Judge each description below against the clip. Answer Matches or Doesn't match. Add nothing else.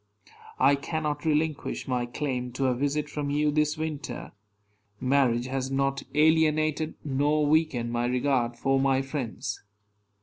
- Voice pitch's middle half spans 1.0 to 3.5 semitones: Matches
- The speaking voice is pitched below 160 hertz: Matches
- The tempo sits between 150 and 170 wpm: Doesn't match